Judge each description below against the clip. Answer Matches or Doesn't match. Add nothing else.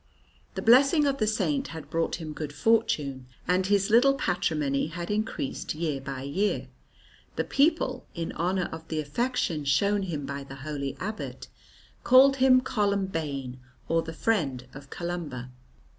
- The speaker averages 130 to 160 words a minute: Matches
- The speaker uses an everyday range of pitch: Doesn't match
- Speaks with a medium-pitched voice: Matches